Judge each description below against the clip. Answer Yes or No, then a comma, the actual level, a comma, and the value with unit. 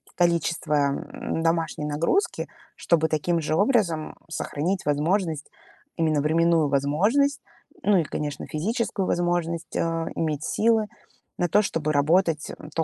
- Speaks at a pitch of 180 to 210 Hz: No, medium, 165 Hz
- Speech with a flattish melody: No, average, 3.2 semitones